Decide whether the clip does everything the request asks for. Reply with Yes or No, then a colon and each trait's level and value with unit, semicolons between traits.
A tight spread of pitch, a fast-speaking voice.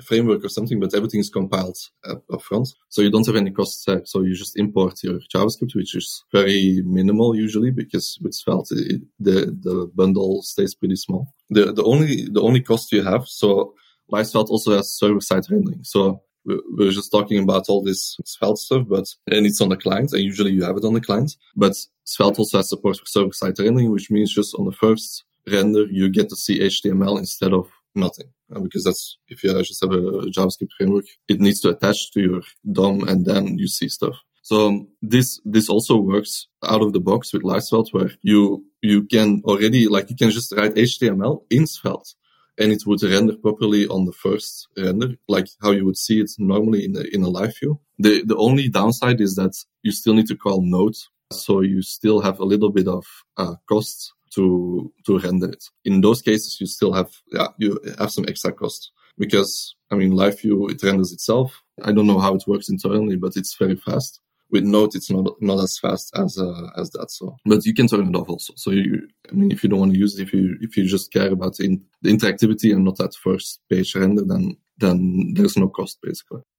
Yes: narrow, 2.2 semitones; fast, 215 wpm